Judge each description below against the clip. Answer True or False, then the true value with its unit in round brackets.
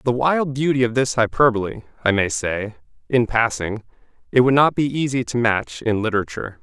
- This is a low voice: True (120 Hz)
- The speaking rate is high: False (180 wpm)